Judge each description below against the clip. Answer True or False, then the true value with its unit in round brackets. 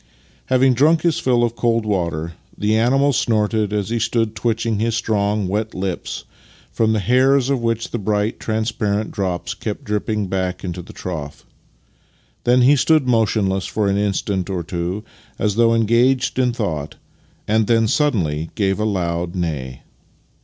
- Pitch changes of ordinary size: True (3.7 semitones)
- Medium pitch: False (105 Hz)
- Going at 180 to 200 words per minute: False (160 wpm)